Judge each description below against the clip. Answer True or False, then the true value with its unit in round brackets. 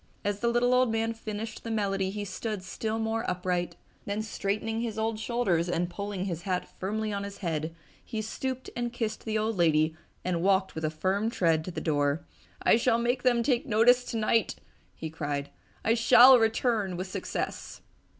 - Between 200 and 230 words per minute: False (185 wpm)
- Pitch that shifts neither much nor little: True (3.9 semitones)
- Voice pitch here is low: False (210 Hz)